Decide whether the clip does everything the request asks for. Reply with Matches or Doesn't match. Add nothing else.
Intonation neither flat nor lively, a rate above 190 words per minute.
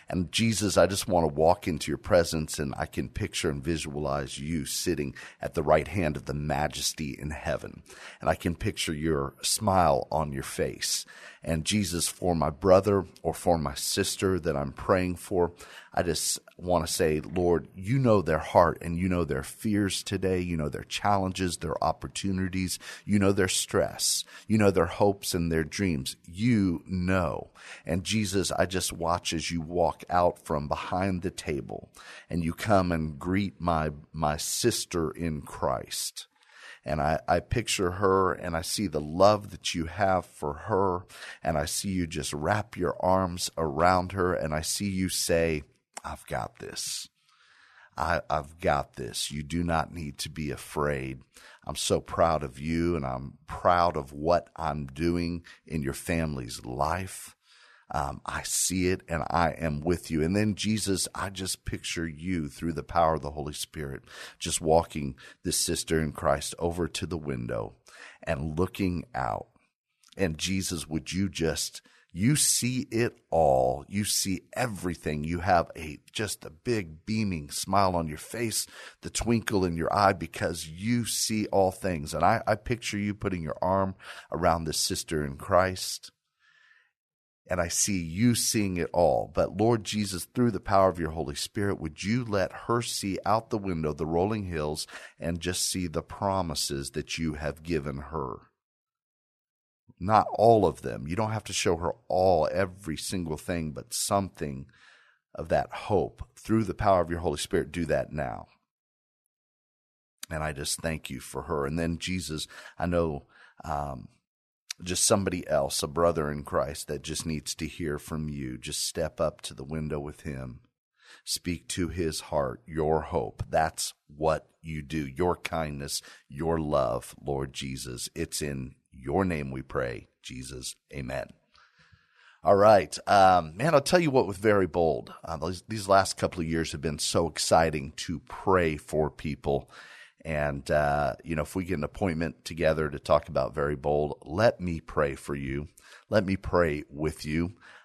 Doesn't match